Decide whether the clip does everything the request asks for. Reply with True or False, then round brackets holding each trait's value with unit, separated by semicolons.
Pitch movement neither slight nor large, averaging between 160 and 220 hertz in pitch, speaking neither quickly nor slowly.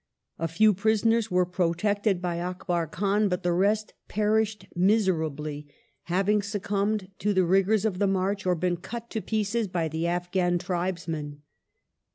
True (3.0 semitones; 190 Hz; 155 wpm)